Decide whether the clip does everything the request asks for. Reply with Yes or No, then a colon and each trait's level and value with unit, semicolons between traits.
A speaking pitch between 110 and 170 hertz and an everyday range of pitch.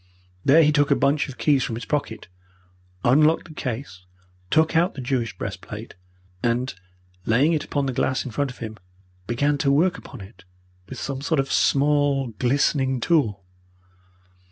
Yes: low, 135 Hz; average, 3.6 semitones